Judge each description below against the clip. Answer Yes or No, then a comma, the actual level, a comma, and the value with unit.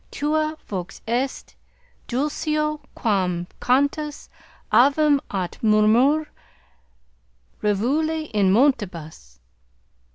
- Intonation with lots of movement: Yes, wide, 6.8 semitones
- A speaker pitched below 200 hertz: No, very high, 255 Hz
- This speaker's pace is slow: Yes, slow, 70 wpm